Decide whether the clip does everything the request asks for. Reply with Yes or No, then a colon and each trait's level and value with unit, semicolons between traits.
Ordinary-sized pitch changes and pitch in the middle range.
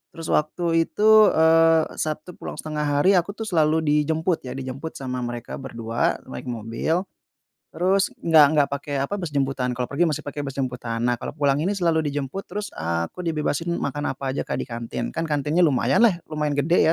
Yes: average, 3.6 semitones; medium, 150 Hz